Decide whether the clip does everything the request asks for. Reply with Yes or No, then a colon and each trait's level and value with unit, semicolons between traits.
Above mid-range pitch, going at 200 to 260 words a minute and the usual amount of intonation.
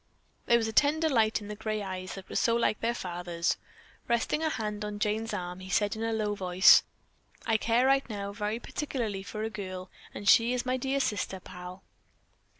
Yes: high, 215 Hz; fast, 205 wpm; average, 3.4 semitones